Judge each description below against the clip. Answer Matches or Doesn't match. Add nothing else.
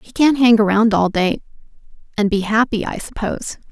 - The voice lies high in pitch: Matches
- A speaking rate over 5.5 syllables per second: Doesn't match